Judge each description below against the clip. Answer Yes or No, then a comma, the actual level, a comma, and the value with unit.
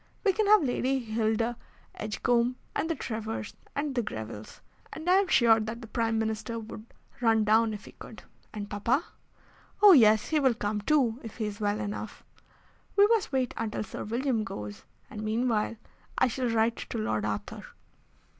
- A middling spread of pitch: Yes, average, 3.1 semitones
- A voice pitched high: Yes, high, 225 Hz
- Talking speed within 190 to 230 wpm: No, average, 175 wpm